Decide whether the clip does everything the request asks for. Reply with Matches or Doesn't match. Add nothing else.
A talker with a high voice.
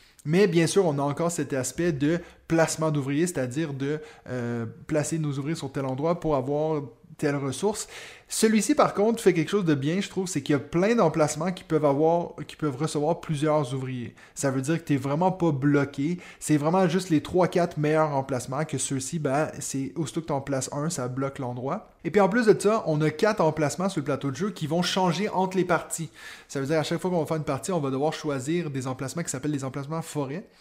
Doesn't match